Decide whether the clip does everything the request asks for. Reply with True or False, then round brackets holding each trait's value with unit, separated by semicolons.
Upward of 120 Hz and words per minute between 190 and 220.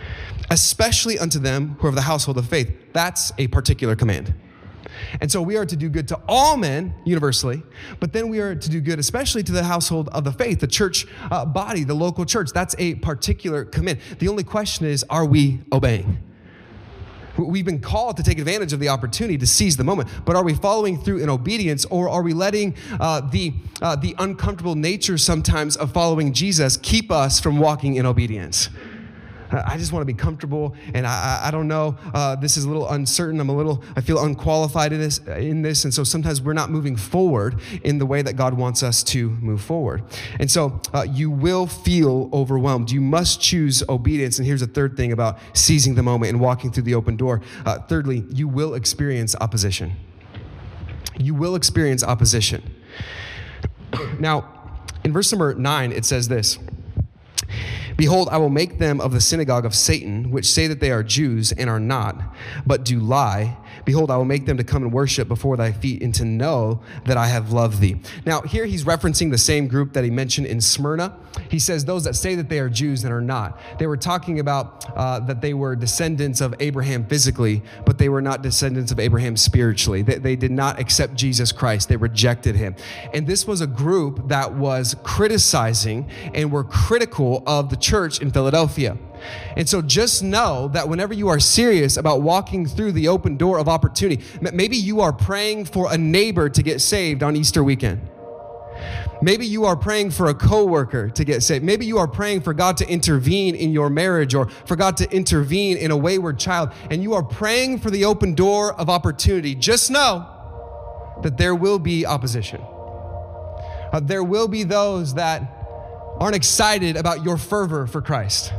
True (140 Hz; 195 wpm)